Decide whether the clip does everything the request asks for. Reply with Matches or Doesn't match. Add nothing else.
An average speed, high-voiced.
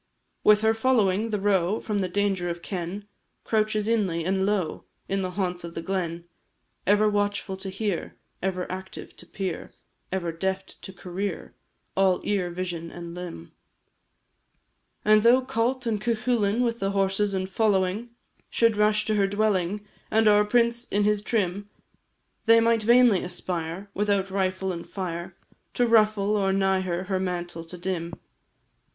Matches